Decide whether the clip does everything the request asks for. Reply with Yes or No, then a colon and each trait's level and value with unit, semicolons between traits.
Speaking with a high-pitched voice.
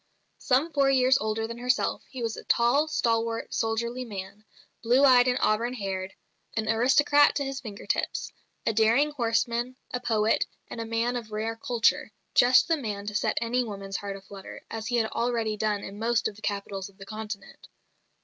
Yes: high, 230 Hz